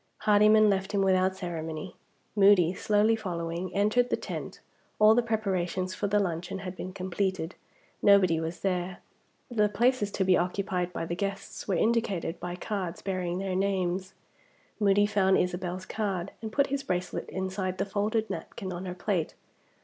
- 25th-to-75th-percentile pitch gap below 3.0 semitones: Yes, narrow, 2.4 semitones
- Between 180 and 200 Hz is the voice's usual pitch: Yes, high, 190 Hz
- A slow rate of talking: No, average, 160 wpm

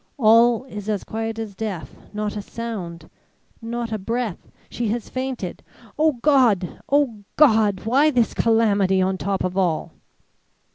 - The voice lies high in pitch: Yes, high, 220 Hz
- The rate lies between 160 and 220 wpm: No, average, 145 wpm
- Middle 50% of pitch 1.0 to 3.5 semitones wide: Yes, average, 3.2 semitones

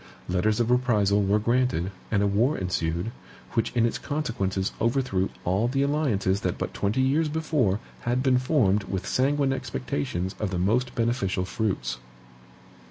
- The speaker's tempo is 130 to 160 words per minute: Yes, average, 155 wpm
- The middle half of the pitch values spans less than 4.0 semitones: No, average, 5.1 semitones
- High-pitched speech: No, low, 110 Hz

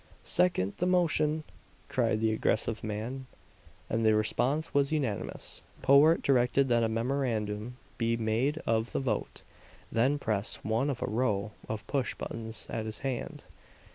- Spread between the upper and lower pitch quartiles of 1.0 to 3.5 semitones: No, average, 3.9 semitones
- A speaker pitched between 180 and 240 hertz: No, low, 115 Hz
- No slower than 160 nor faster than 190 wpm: No, average, 140 wpm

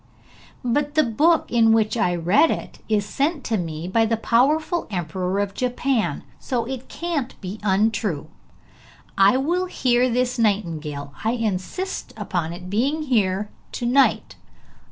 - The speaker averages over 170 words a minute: No, average, 145 wpm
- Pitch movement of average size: No, wide, 5.8 semitones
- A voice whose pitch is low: No, high, 225 Hz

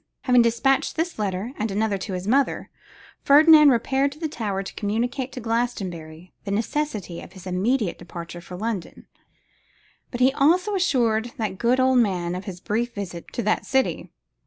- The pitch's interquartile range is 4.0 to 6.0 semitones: Yes, wide, 5.6 semitones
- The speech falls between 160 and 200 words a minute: Yes, average, 170 wpm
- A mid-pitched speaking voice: No, high, 225 Hz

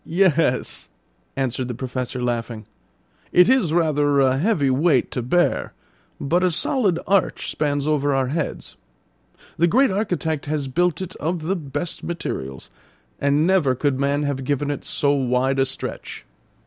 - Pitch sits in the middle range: Yes, medium, 145 Hz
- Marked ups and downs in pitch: No, average, 4.5 semitones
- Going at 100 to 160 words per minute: Yes, average, 150 wpm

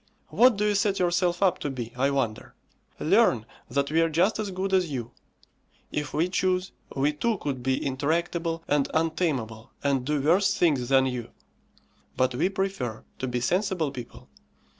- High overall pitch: No, medium, 155 Hz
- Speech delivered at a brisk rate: No, average, 170 wpm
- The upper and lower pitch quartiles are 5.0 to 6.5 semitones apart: Yes, wide, 5.6 semitones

